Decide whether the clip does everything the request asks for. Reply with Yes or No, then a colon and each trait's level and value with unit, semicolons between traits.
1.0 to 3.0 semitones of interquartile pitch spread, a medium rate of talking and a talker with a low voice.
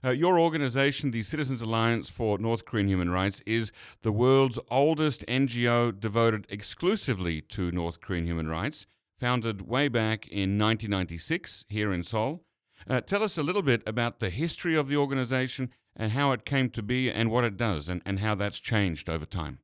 No: average, 4.5 semitones; average, 185 wpm; low, 115 Hz